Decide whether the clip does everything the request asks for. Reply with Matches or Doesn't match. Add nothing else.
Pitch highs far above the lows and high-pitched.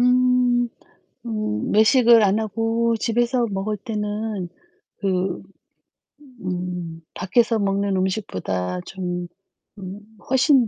Doesn't match